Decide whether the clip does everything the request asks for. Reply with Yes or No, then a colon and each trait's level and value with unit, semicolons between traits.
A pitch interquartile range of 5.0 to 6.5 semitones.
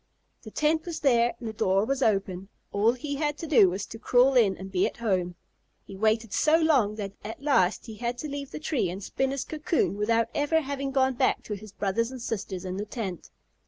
Yes: wide, 5.6 semitones